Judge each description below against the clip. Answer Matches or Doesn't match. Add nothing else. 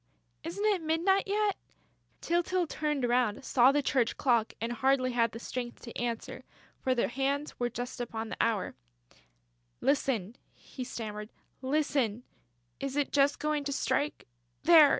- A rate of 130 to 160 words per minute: Matches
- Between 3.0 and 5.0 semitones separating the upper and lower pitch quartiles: Matches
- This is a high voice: Matches